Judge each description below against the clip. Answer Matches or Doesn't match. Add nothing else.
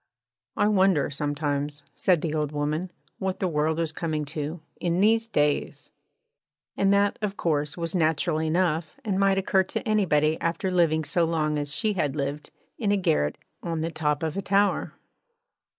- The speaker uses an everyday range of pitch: Matches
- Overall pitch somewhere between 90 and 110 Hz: Doesn't match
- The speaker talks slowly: Doesn't match